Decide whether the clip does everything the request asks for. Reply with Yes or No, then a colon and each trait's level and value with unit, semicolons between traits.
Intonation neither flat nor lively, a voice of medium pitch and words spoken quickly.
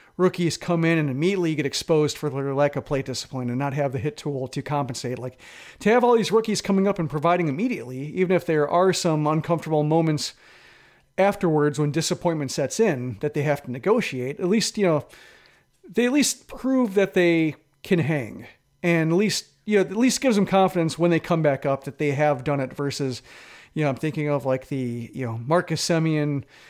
Yes: average, 4.5 semitones; medium, 155 Hz; fast, 210 wpm